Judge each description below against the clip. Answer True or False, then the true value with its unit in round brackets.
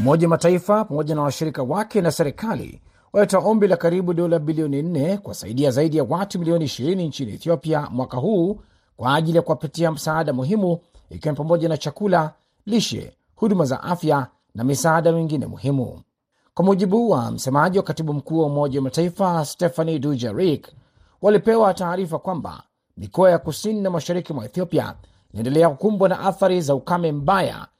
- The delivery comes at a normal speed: False (160 wpm)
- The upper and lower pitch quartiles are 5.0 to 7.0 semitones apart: False (4.1 semitones)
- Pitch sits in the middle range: True (165 Hz)